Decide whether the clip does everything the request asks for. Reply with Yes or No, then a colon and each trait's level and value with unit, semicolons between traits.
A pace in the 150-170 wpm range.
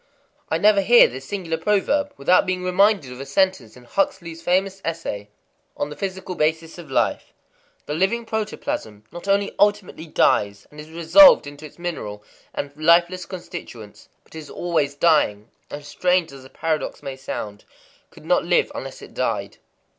Yes: average, 165 wpm